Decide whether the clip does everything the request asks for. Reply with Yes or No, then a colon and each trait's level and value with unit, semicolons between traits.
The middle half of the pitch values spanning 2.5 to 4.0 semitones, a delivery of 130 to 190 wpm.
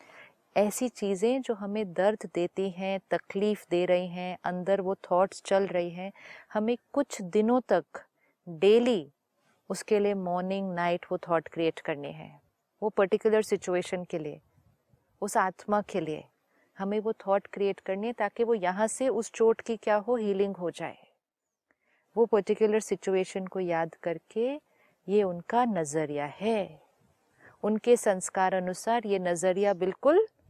Yes: average, 3.3 semitones; average, 145 wpm